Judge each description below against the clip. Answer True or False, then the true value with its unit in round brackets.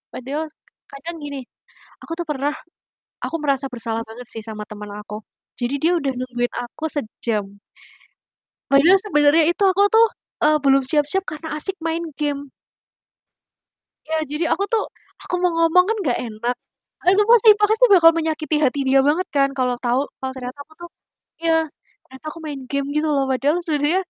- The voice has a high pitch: True (290 Hz)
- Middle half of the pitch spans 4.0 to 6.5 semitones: True (4.4 semitones)